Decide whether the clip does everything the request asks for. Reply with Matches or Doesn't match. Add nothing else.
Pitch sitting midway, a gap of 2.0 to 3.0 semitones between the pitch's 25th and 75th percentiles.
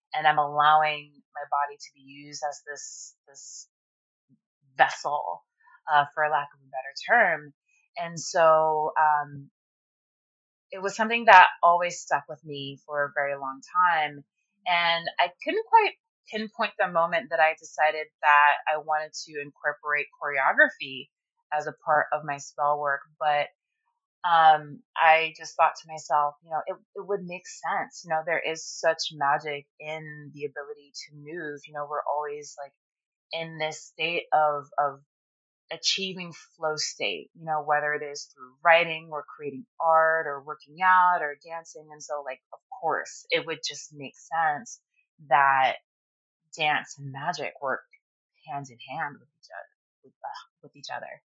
Matches